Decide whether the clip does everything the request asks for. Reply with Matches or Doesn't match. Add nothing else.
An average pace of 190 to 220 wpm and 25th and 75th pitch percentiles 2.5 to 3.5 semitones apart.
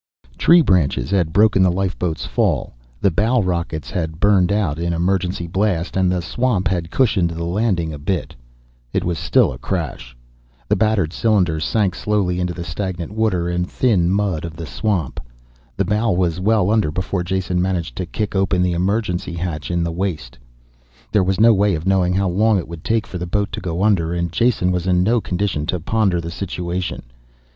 Matches